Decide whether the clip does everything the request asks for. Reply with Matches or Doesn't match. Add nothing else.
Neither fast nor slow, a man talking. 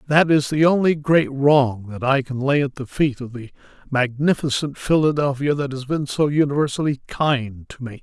Matches